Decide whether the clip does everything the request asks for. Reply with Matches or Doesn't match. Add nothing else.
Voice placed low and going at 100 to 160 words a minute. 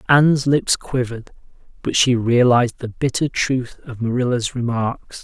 Matches